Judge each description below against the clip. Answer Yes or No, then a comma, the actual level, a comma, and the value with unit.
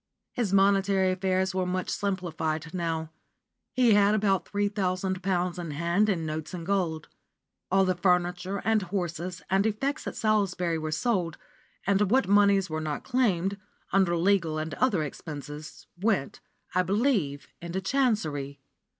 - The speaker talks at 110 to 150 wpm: Yes, average, 145 wpm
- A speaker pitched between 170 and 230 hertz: Yes, medium, 185 Hz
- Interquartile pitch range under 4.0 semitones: Yes, average, 3.1 semitones